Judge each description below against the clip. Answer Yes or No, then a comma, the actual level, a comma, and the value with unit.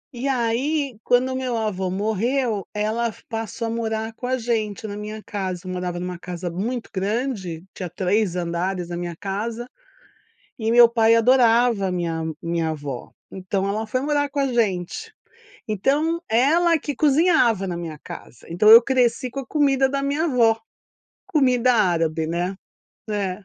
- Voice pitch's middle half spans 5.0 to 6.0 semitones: Yes, wide, 5.6 semitones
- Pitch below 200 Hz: No, high, 220 Hz